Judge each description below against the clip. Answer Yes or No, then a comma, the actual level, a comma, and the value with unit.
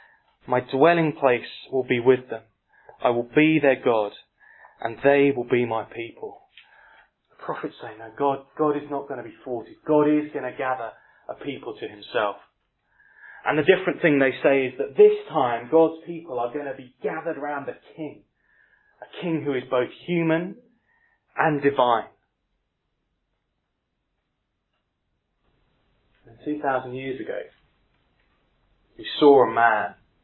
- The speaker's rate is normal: Yes, average, 150 wpm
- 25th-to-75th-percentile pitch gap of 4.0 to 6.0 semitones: Yes, average, 4.8 semitones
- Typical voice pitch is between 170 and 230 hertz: No, medium, 140 Hz